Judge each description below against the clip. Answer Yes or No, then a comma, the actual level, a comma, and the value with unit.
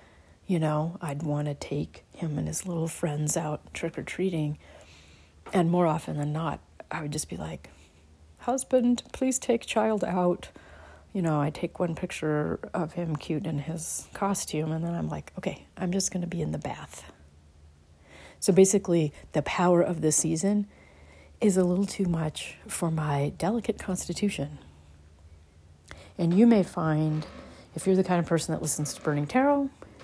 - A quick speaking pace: No, average, 170 wpm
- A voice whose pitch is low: No, medium, 160 Hz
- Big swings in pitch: No, average, 3.9 semitones